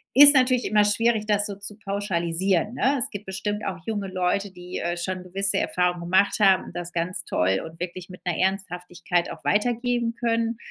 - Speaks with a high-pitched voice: Yes, high, 195 Hz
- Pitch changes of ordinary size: Yes, average, 3.2 semitones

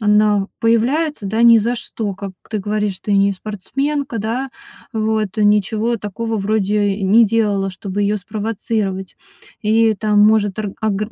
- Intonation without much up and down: Yes, narrow, 2.0 semitones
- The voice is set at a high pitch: Yes, high, 210 Hz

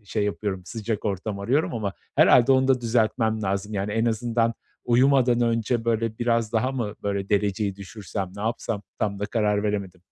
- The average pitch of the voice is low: Yes, low, 110 Hz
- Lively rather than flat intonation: No, narrow, 2.6 semitones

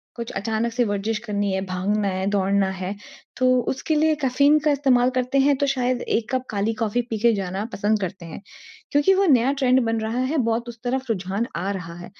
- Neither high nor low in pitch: No, high, 225 Hz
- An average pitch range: Yes, average, 4.4 semitones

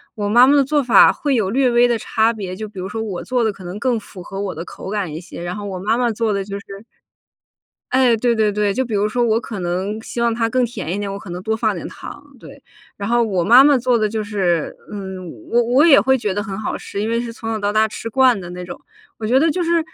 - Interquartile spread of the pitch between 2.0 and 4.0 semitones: Yes, average, 3.3 semitones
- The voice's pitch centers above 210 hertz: Yes, high, 220 Hz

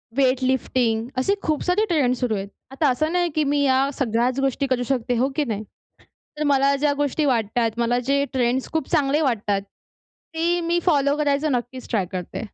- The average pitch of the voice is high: Yes, very high, 270 Hz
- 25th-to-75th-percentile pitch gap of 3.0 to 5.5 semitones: Yes, average, 3.3 semitones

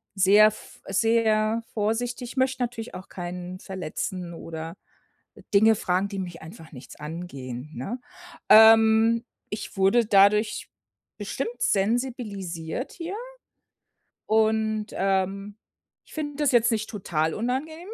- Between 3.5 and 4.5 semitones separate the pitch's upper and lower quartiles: Yes, average, 4.0 semitones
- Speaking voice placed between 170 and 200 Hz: No, high, 210 Hz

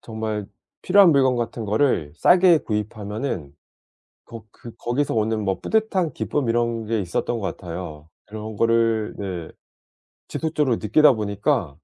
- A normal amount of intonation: Yes, average, 4.5 semitones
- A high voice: No, low, 110 Hz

